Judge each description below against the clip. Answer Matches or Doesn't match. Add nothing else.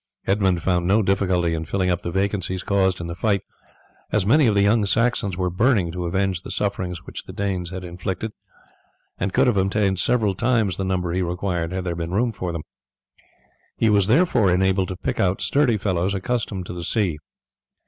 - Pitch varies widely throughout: Doesn't match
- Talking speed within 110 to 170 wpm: Doesn't match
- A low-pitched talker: Matches